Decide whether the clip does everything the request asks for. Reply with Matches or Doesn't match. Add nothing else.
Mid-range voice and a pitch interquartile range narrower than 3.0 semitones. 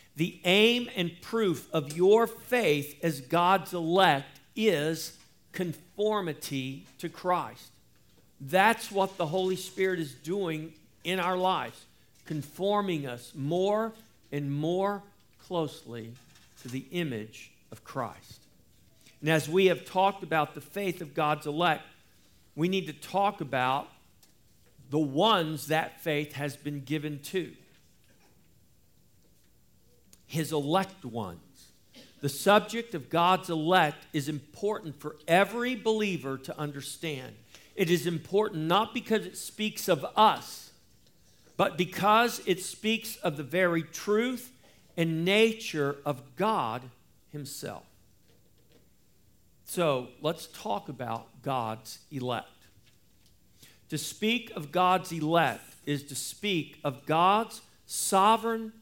Doesn't match